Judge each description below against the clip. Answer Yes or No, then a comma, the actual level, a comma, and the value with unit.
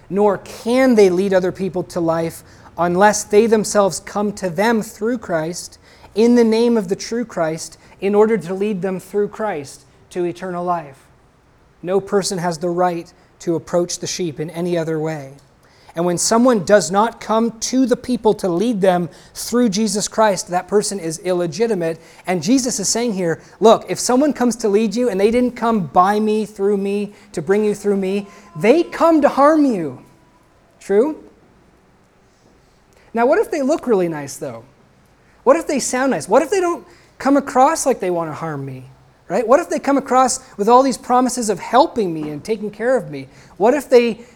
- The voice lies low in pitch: No, high, 205 Hz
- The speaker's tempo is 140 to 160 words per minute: No, average, 190 wpm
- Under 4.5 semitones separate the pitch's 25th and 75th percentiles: No, average, 5.1 semitones